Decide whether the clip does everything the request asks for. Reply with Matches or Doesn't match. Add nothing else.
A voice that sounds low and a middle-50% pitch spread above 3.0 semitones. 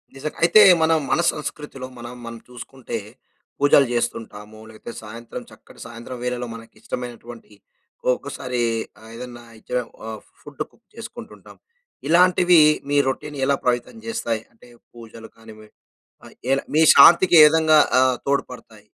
Matches